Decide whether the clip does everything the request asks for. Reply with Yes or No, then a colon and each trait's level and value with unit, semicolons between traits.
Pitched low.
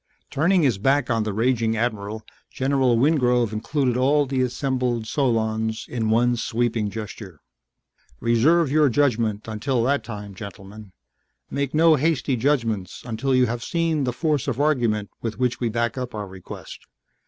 Yes: low, 120 Hz